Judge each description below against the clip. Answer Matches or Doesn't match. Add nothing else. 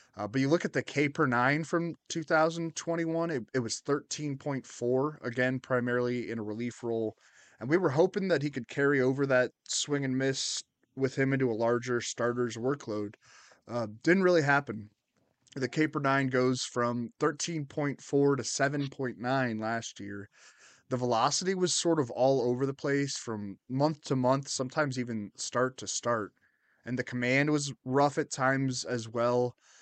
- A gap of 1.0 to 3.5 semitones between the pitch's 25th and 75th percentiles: Matches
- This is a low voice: Matches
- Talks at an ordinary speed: Matches